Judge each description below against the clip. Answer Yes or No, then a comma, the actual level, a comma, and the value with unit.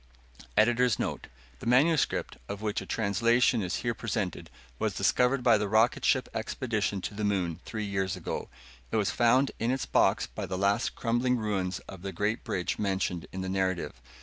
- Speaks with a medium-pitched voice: No, low, 105 Hz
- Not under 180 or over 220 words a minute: Yes, average, 185 wpm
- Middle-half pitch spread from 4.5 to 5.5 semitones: No, average, 3.8 semitones